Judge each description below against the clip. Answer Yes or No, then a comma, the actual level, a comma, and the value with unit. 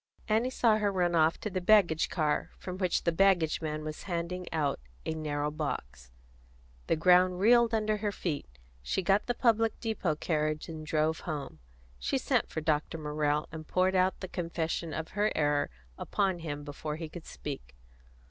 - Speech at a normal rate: Yes, average, 175 wpm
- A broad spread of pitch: No, average, 3.8 semitones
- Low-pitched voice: No, medium, 165 Hz